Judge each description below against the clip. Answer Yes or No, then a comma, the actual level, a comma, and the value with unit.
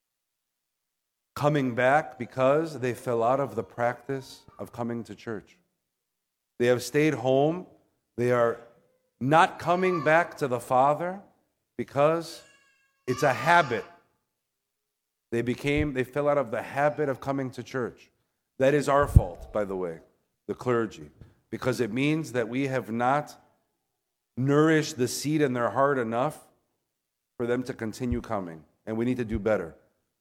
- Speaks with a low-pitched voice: Yes, low, 130 Hz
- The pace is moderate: Yes, average, 150 wpm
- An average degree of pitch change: Yes, average, 3.8 semitones